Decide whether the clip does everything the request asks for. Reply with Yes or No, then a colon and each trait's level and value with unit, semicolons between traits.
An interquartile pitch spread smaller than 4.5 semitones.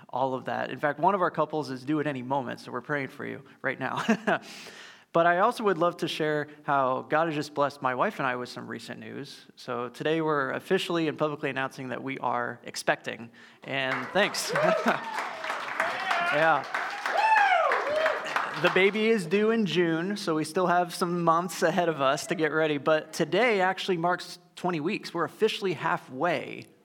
Yes: average, 3.5 semitones